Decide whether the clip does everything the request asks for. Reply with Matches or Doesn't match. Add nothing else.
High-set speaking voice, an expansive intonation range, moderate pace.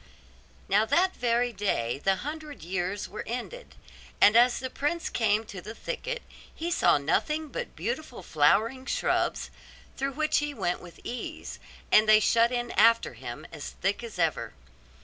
Matches